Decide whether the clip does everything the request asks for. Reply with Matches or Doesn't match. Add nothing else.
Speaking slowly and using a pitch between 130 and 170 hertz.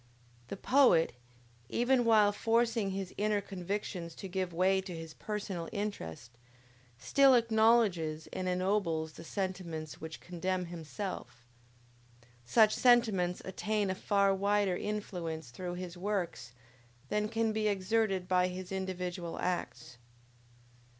Doesn't match